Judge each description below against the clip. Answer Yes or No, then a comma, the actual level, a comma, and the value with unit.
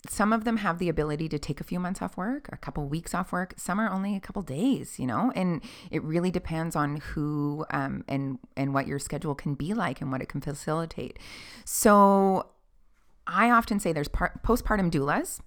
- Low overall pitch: No, medium, 165 Hz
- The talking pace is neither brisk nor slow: No, fast, 210 wpm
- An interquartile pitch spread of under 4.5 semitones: No, average, 5.2 semitones